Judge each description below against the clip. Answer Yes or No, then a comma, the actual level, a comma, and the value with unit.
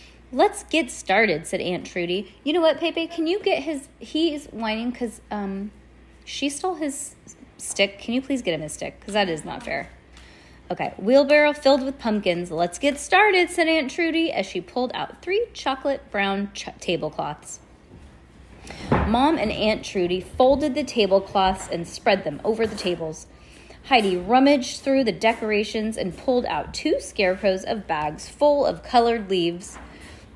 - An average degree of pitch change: No, wide, 7.6 semitones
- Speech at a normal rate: Yes, average, 165 wpm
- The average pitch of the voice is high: Yes, high, 230 Hz